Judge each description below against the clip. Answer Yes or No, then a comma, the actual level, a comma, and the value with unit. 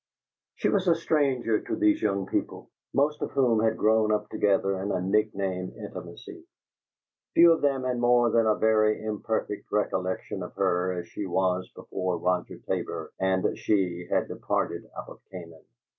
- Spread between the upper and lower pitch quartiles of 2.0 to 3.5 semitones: No, average, 3.9 semitones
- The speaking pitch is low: Yes, low, 105 Hz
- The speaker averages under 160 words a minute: No, average, 165 wpm